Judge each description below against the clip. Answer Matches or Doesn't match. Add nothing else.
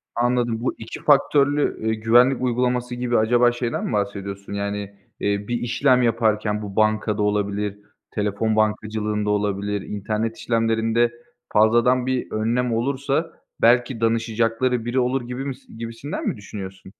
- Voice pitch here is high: Doesn't match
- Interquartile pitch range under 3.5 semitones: Matches